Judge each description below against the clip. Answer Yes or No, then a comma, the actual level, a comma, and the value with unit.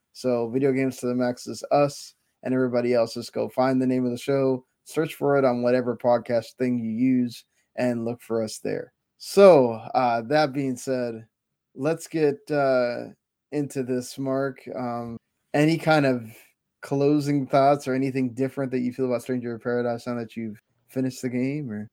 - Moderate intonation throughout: No, narrow, 2.3 semitones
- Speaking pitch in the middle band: No, low, 130 Hz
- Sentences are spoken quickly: No, average, 185 wpm